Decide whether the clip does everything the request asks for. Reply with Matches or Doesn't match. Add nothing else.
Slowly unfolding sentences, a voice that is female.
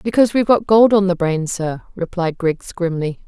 Doesn't match